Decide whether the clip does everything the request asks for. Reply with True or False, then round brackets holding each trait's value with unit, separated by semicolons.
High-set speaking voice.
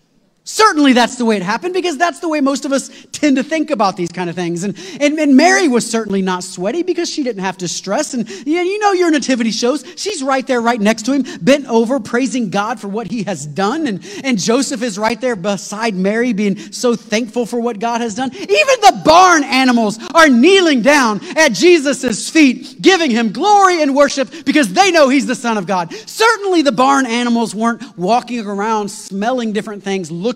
True (245 Hz)